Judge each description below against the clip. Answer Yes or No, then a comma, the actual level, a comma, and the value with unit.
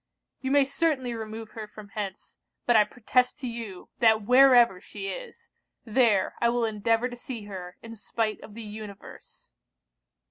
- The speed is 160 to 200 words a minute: Yes, average, 165 wpm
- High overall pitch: Yes, high, 225 Hz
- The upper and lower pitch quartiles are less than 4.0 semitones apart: Yes, average, 2.7 semitones